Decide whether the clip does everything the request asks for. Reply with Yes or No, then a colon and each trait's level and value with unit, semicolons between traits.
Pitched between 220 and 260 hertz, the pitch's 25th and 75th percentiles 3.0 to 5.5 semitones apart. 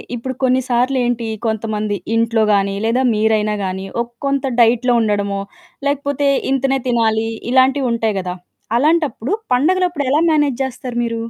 Yes: high, 240 Hz; average, 3.6 semitones